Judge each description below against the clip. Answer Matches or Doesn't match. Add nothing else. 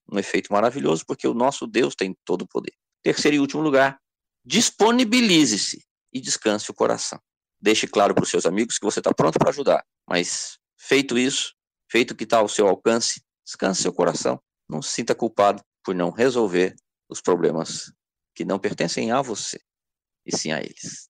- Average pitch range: Doesn't match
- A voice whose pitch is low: Matches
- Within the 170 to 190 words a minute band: Matches